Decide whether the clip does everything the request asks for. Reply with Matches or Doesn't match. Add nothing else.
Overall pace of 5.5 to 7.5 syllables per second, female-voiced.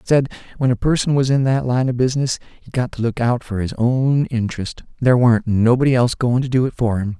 Doesn't match